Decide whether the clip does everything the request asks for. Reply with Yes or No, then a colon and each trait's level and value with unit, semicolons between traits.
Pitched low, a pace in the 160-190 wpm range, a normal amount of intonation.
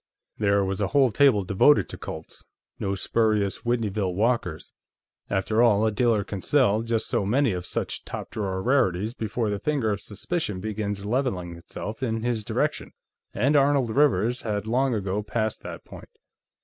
Yes: low, 110 Hz; average, 165 wpm; average, 3.4 semitones